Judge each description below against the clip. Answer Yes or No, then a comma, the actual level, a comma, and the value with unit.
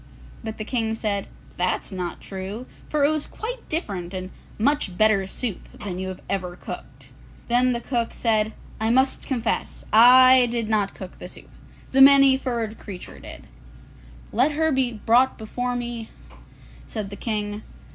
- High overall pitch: Yes, high, 225 Hz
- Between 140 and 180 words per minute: Yes, average, 160 wpm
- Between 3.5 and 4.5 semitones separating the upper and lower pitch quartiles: Yes, average, 4.1 semitones